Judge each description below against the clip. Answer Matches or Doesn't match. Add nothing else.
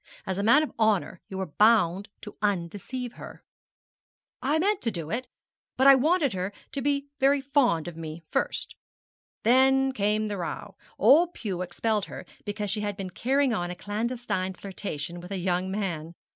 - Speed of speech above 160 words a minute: Matches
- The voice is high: Matches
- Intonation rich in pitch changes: Matches